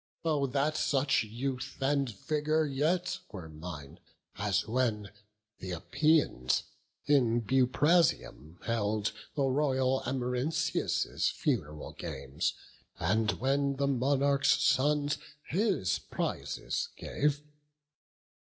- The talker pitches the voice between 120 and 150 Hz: Yes, low, 135 Hz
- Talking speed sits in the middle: No, slow, 95 wpm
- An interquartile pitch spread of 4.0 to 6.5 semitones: Yes, average, 5.2 semitones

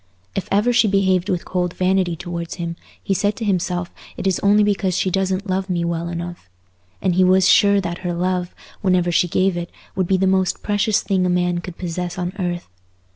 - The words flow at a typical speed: No, fast, 210 wpm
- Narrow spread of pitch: Yes, narrow, 1.7 semitones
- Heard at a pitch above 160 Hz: Yes, medium, 185 Hz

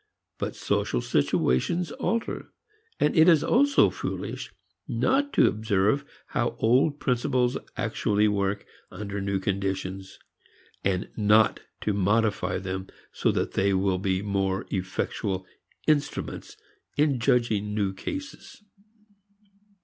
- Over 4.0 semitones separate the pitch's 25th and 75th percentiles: Yes, average, 5.1 semitones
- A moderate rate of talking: No, slow, 110 wpm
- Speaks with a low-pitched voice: Yes, low, 105 Hz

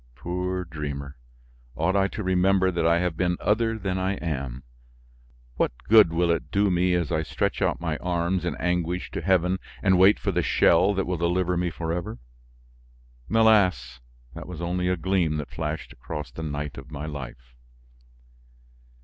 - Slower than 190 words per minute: Yes, average, 170 wpm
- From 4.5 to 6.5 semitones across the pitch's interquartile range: No, average, 3.0 semitones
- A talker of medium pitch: No, very low, 90 Hz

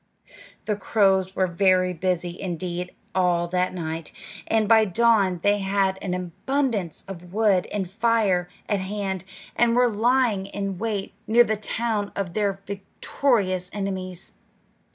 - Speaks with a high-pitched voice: Yes, high, 195 Hz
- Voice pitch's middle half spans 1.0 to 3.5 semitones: Yes, average, 2.9 semitones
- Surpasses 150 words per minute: No, slow, 135 wpm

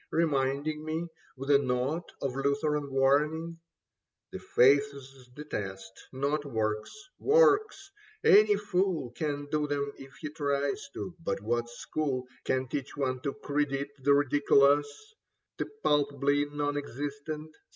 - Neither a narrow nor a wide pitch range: No, narrow, 2.2 semitones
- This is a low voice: No, medium, 145 Hz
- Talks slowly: Yes, slow, 130 wpm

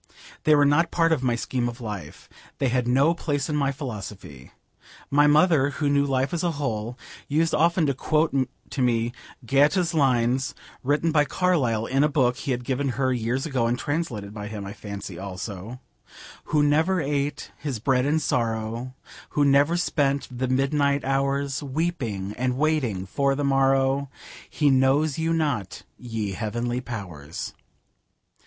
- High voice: No, low, 135 Hz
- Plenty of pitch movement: No, average, 3.7 semitones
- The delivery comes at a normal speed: Yes, average, 160 wpm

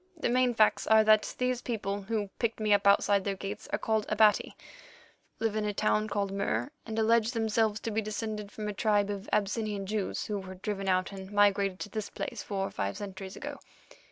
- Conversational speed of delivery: No, fast, 210 wpm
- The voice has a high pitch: Yes, high, 210 Hz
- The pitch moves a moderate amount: No, narrow, 1.7 semitones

